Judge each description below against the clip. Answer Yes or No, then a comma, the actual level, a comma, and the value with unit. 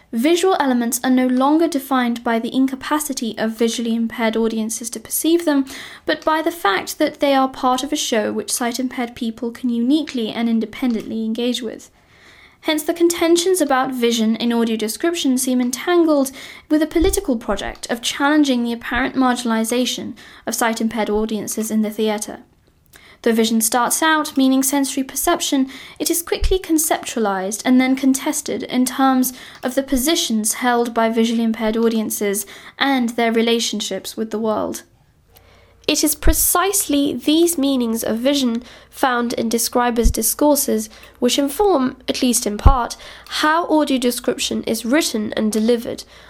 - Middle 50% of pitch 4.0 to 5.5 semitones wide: Yes, average, 4.3 semitones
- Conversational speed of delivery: Yes, average, 150 wpm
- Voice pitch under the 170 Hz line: No, very high, 255 Hz